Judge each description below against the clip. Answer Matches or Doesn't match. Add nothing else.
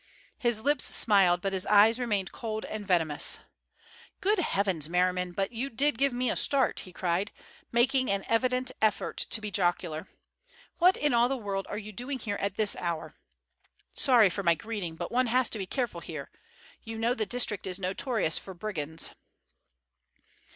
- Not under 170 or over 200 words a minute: Matches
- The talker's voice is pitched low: Doesn't match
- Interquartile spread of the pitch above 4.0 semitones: Matches